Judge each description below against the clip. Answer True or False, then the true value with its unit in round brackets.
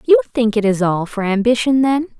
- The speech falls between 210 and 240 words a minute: True (220 wpm)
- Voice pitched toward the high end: True (225 Hz)